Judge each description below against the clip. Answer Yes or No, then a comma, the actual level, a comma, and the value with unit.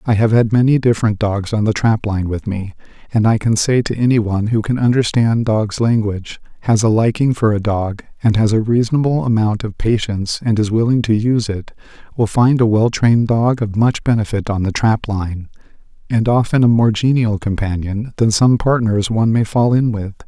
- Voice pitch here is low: Yes, low, 110 Hz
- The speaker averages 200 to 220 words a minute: Yes, fast, 205 wpm